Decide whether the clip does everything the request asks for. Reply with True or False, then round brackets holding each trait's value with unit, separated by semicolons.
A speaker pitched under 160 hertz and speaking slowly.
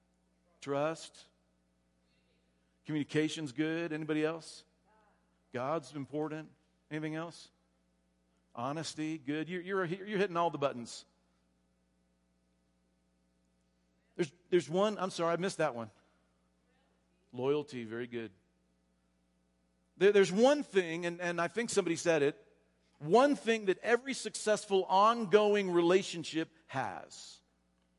True (140 Hz; 105 wpm)